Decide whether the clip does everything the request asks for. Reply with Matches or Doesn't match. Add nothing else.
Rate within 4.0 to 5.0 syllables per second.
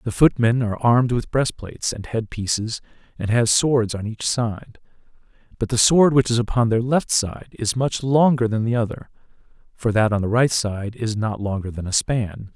Matches